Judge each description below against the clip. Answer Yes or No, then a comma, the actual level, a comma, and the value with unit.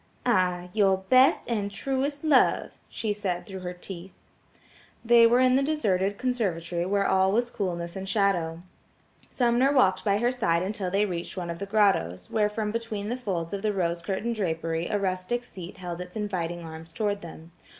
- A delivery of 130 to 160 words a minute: No, average, 180 wpm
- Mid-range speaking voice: No, high, 195 Hz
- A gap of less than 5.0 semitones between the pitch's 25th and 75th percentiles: Yes, average, 4.2 semitones